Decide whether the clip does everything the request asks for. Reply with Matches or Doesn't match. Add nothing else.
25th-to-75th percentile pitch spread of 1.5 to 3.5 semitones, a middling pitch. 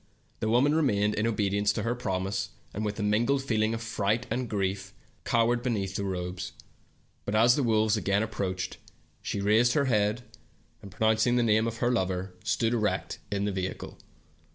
Doesn't match